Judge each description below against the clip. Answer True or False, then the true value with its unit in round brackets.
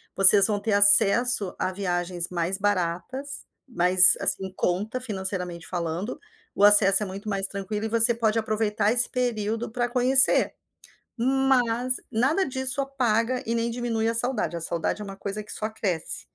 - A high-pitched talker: True (215 Hz)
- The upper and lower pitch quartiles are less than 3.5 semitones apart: False (3.9 semitones)